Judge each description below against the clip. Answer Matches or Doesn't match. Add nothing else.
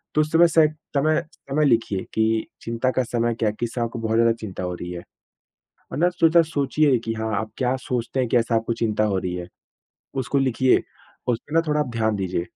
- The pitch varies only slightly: Doesn't match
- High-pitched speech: Doesn't match